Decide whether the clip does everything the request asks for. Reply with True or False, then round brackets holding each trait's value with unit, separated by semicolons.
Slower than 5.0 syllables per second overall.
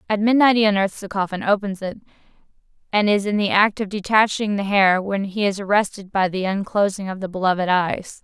False (5.6 syllables/s)